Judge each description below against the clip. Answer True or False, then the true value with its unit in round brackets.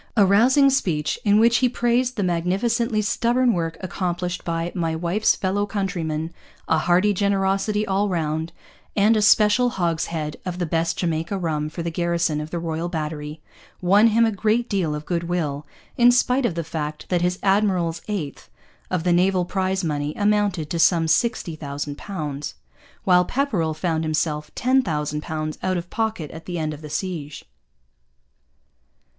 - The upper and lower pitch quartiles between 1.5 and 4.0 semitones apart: False (4.4 semitones)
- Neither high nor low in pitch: True (175 Hz)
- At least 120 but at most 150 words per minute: False (165 wpm)